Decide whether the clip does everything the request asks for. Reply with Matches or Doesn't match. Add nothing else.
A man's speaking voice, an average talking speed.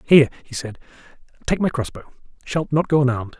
Matches